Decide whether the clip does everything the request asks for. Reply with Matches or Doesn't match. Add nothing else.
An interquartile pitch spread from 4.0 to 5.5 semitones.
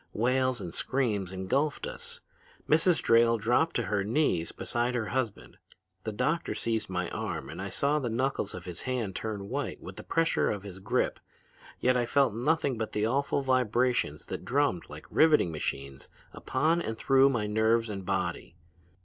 Matches